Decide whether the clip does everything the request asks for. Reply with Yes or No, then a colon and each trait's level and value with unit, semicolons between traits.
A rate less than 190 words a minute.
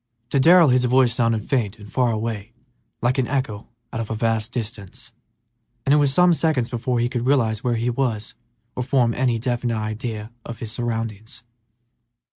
Yes: average, 180 wpm